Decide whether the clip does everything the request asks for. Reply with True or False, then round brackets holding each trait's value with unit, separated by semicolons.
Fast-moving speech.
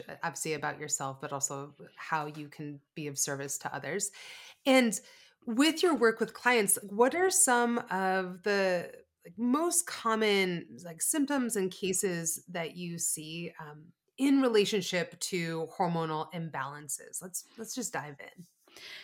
False (140 wpm)